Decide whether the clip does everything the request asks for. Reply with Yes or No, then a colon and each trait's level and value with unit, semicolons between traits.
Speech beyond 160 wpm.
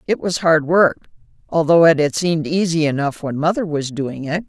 Yes: average, 200 wpm